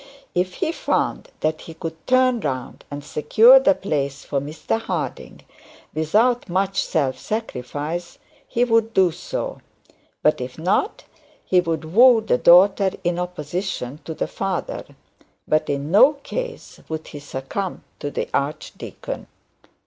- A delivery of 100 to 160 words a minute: Yes, average, 140 wpm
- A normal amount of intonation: No, wide, 6.6 semitones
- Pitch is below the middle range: No, medium, 175 Hz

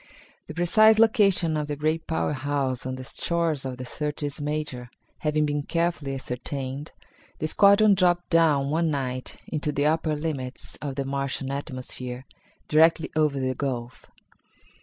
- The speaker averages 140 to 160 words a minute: Yes, average, 150 wpm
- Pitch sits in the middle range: Yes, medium, 150 Hz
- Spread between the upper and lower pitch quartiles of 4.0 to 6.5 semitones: No, average, 3.3 semitones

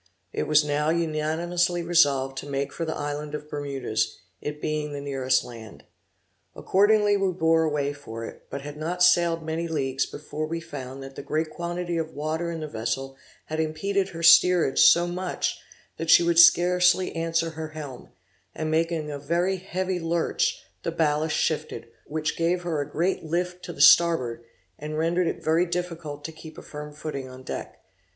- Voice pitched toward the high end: No, medium, 160 Hz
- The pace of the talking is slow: No, average, 180 wpm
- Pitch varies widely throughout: No, average, 2.8 semitones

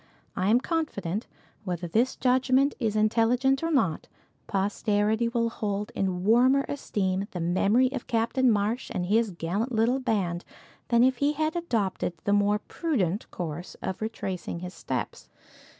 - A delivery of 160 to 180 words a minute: No, average, 150 wpm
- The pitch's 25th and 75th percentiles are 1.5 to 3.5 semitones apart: No, average, 4.9 semitones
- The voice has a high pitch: Yes, high, 220 Hz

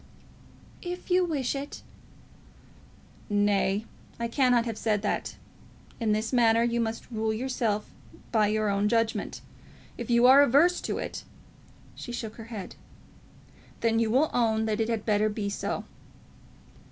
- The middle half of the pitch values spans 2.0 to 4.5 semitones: Yes, narrow, 2.4 semitones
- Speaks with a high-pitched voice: Yes, high, 225 Hz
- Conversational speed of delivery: Yes, average, 150 wpm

